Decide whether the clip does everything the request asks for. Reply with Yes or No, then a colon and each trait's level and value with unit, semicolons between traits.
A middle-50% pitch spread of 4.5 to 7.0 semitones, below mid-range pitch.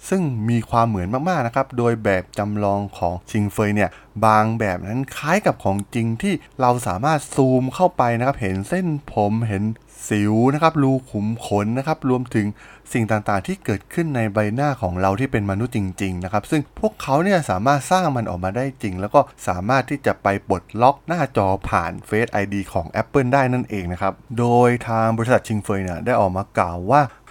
Yes: average, 5.1 semitones; low, 115 Hz